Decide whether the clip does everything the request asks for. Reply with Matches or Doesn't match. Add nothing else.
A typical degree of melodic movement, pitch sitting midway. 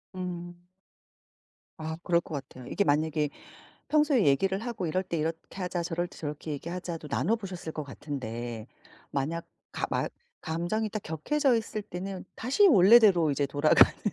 Matches